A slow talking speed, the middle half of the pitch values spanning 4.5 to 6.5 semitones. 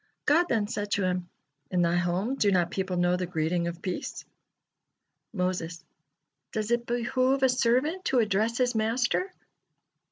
No: average, 155 wpm; wide, 5.4 semitones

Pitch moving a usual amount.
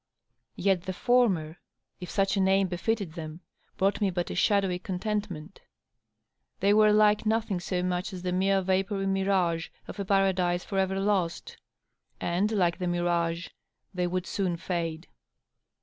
No: narrow, 2.2 semitones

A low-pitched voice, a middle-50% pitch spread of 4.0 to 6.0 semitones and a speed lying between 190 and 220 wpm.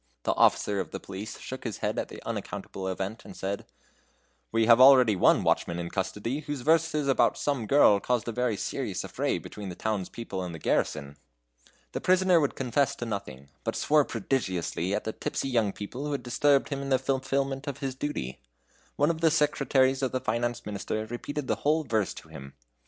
Yes: low, 120 Hz; wide, 5.5 semitones; average, 200 wpm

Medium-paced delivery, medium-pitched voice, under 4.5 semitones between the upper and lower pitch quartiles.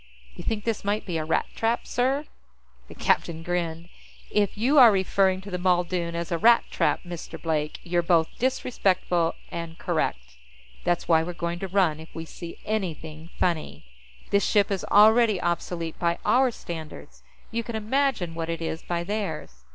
Yes: average, 175 wpm; medium, 175 Hz; average, 4.1 semitones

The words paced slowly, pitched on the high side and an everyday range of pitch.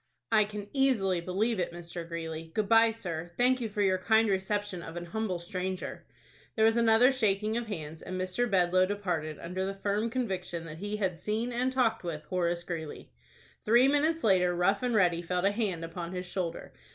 No: average, 195 wpm; high, 195 Hz; average, 4.2 semitones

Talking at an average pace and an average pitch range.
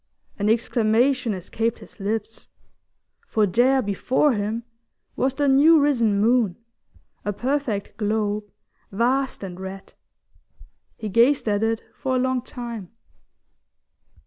No: slow, 120 wpm; average, 3.9 semitones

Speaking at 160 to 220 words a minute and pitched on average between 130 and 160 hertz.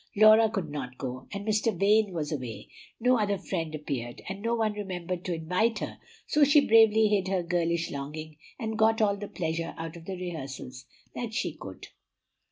No: average, 185 wpm; medium, 185 Hz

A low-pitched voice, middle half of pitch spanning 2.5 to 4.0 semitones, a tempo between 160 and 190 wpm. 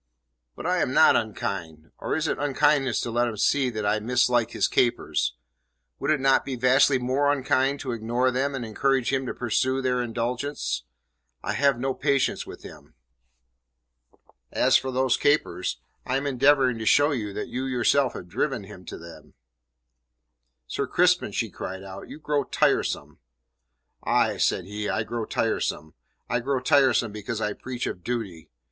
Yes: low, 125 Hz; average, 3.6 semitones; average, 170 wpm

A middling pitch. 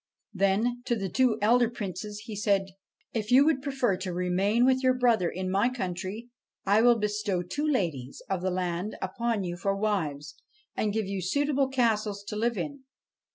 No: high, 210 Hz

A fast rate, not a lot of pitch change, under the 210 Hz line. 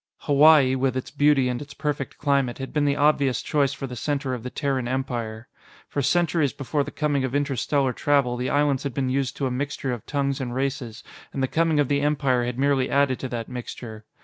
Yes: fast, 220 wpm; narrow, 2.1 semitones; low, 135 Hz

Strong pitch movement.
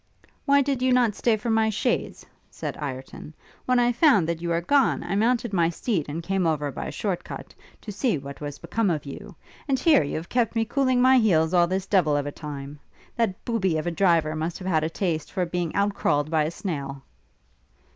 Yes: wide, 6.5 semitones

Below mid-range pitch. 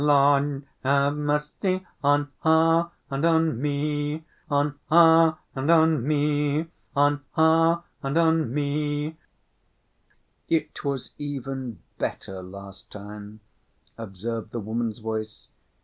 No: medium, 145 Hz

